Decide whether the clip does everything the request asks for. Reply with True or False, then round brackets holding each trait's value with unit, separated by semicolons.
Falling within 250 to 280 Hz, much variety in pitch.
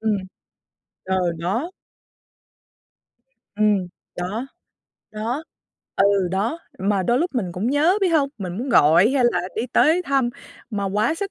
False (220 Hz; 6.6 semitones)